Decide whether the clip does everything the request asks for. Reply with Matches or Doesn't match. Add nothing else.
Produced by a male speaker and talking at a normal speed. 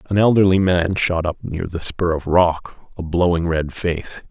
Matches